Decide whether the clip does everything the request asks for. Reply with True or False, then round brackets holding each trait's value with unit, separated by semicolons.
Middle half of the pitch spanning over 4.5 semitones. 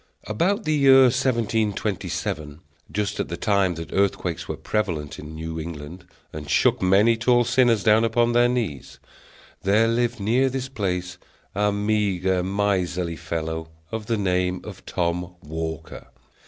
True (4.9 semitones)